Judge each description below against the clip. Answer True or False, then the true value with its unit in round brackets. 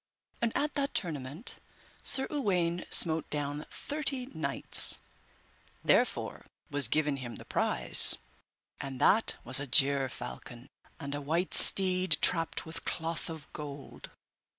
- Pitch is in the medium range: True (155 Hz)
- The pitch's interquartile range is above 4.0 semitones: True (4.7 semitones)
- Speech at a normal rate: False (125 wpm)